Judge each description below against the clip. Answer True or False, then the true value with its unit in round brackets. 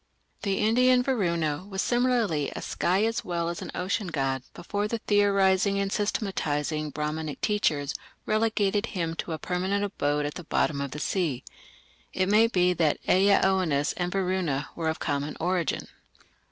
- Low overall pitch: False (185 Hz)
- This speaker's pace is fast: False (160 wpm)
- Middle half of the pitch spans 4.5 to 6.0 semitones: True (4.8 semitones)